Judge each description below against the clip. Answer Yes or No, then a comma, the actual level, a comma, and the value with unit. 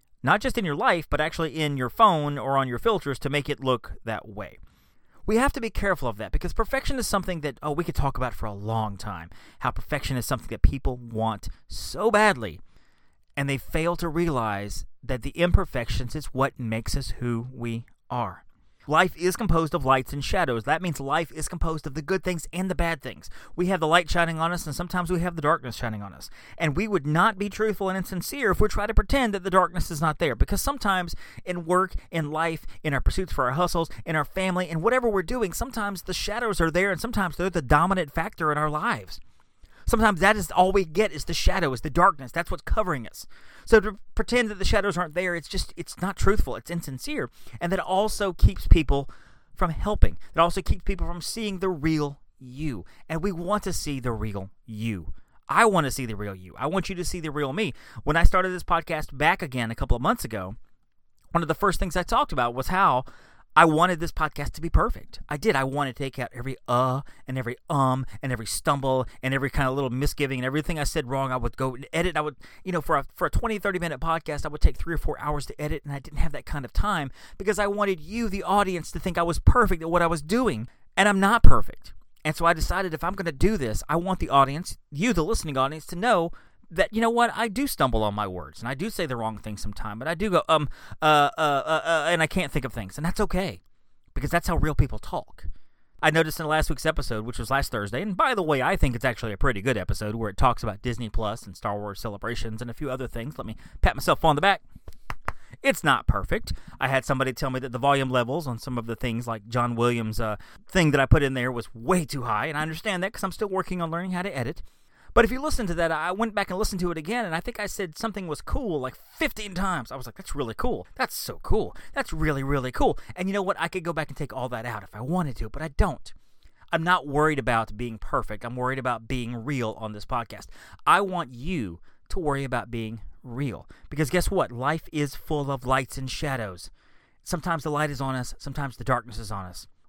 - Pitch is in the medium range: Yes, medium, 150 Hz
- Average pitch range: No, wide, 6.3 semitones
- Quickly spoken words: Yes, fast, 250 wpm